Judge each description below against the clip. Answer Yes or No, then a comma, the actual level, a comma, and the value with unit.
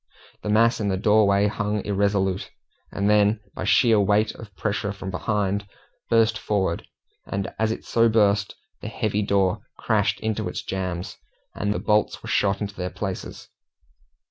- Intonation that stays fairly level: Yes, narrow, 1.6 semitones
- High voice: No, low, 105 Hz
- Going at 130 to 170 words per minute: Yes, average, 160 wpm